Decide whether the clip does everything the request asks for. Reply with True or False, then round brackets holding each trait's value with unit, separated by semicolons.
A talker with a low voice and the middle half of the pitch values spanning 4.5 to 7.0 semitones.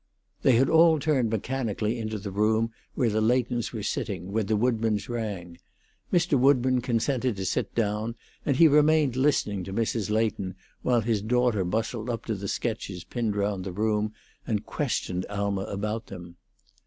False (110 Hz; 3.4 semitones)